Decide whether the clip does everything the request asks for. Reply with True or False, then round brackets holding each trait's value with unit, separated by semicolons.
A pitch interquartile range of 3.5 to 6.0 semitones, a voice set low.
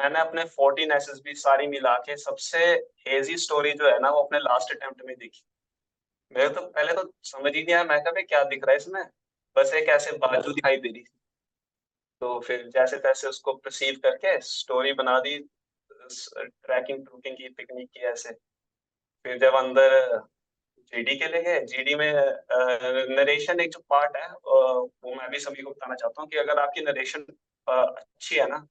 False (4.6 semitones; 145 Hz)